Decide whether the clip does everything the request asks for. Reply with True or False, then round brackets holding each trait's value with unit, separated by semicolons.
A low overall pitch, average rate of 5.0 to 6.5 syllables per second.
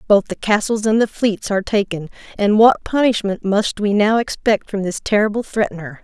False (210 Hz; 5.2 syllables/s)